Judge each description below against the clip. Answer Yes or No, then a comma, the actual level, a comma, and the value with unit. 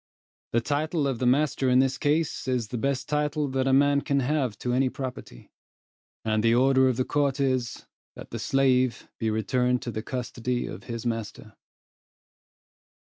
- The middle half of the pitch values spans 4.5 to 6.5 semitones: No, narrow, 2.4 semitones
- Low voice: Yes, low, 130 Hz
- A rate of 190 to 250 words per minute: No, average, 175 wpm